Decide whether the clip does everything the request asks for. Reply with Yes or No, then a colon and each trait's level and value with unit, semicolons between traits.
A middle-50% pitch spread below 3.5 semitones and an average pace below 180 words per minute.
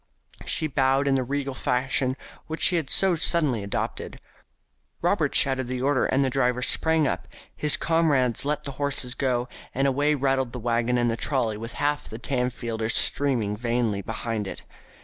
Yes: average, 2.9 semitones; average, 170 wpm